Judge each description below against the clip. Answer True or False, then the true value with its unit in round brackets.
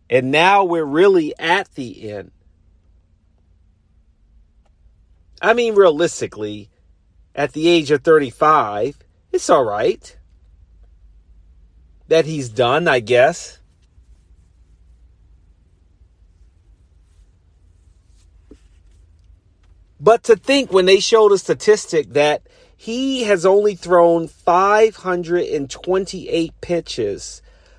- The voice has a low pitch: True (95 Hz)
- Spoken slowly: True (80 wpm)